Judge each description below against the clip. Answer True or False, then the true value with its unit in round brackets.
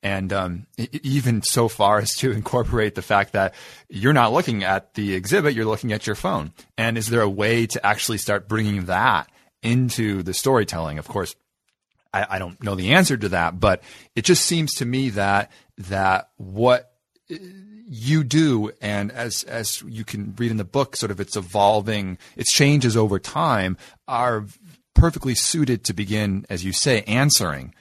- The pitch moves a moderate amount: True (4.0 semitones)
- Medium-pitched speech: False (110 Hz)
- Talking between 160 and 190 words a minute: True (175 wpm)